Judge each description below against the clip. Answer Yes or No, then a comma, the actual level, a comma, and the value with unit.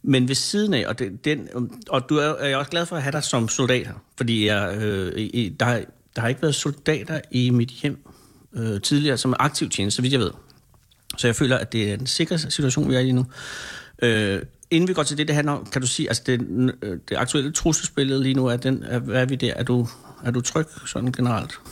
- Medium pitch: No, low, 130 Hz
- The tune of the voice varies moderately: Yes, average, 3.4 semitones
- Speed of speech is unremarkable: No, fast, 250 wpm